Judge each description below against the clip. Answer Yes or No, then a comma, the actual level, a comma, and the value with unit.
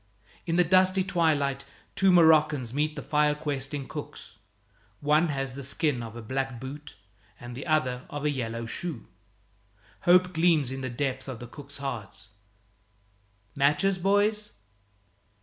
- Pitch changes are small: No, average, 3.8 semitones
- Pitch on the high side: No, medium, 145 Hz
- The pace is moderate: Yes, average, 145 wpm